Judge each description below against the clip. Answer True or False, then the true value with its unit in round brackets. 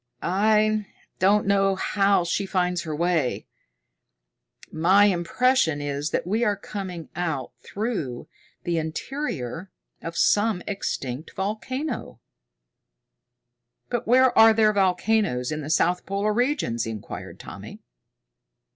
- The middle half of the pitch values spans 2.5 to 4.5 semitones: False (4.9 semitones)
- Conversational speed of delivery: False (110 wpm)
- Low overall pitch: False (190 Hz)